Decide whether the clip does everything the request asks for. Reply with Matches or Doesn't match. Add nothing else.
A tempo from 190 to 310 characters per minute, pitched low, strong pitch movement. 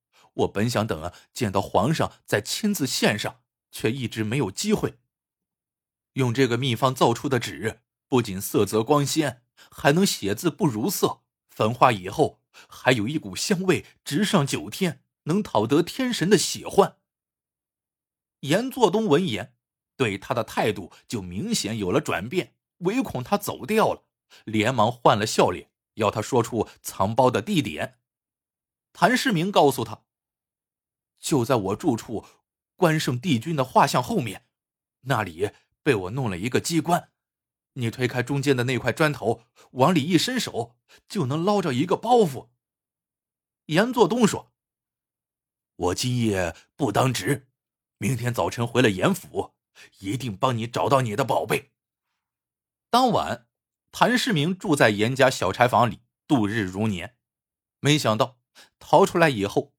Matches